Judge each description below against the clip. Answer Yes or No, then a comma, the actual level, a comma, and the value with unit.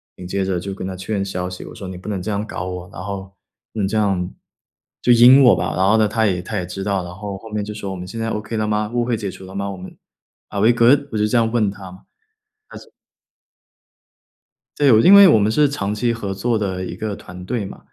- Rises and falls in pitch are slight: No, average, 3.0 semitones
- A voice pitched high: No, low, 100 Hz